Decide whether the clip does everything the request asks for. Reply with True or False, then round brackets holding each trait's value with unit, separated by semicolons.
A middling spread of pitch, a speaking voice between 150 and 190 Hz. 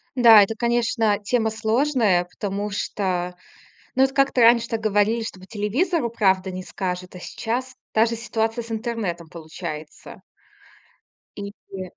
False (3.8 semitones; 220 Hz)